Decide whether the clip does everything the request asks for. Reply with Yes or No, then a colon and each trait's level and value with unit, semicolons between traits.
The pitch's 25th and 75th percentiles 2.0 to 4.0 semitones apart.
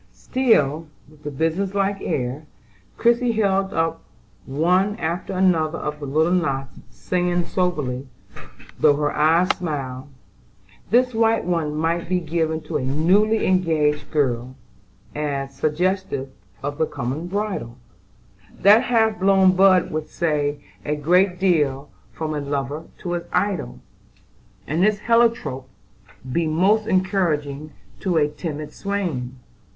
No: average, 4.4 semitones